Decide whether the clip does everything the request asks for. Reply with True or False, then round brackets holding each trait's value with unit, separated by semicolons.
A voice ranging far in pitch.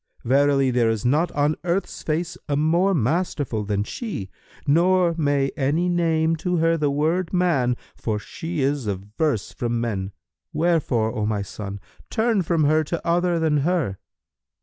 True (6.0 semitones)